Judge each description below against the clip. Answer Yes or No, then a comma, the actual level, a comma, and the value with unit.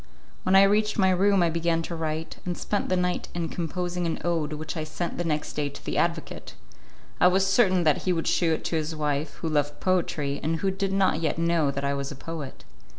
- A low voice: No, medium, 165 Hz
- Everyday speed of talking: No, fast, 235 wpm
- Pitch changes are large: No, average, 3.1 semitones